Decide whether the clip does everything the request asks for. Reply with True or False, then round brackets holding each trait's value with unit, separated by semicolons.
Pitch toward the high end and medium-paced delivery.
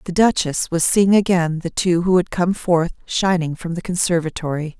False (175 Hz; 190 wpm)